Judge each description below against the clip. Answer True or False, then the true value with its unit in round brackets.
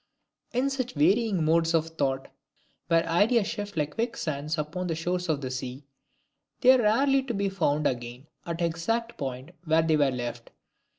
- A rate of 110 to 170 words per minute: False (180 wpm)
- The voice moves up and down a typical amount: False (6.1 semitones)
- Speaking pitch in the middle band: True (165 Hz)